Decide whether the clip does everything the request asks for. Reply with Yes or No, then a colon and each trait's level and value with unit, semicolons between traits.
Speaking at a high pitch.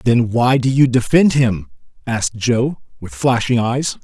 No: low, 120 Hz